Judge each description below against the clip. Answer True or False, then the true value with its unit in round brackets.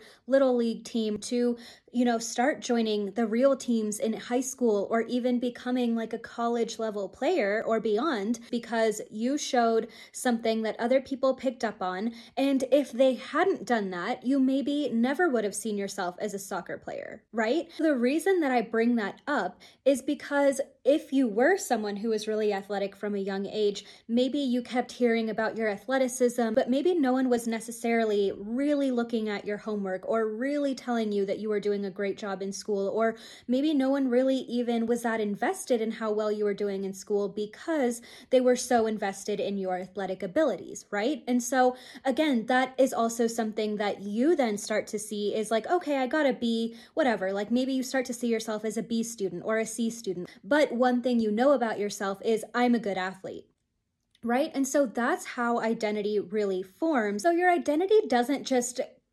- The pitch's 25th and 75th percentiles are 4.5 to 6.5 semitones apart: False (3.5 semitones)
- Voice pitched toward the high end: True (235 Hz)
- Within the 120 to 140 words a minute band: False (195 wpm)